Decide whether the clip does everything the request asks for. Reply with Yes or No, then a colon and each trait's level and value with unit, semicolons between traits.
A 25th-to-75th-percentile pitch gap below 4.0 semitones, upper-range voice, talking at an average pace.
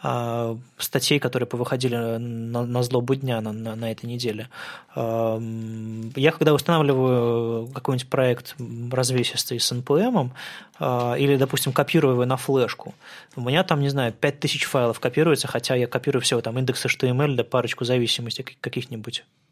No: average, 2.7 semitones; low, 125 Hz; average, 140 wpm